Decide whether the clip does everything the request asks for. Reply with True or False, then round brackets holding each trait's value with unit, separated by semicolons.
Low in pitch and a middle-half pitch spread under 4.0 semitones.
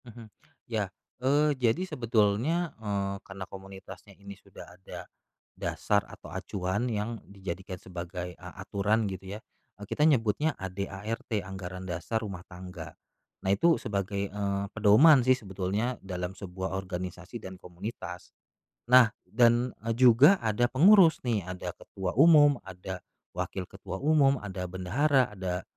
False (100 Hz; 4.3 semitones)